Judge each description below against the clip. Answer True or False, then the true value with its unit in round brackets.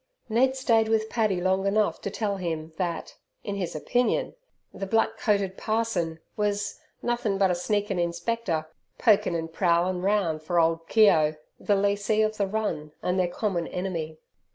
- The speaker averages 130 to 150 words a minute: False (160 wpm)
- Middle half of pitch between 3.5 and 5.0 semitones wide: True (3.9 semitones)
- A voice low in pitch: False (195 Hz)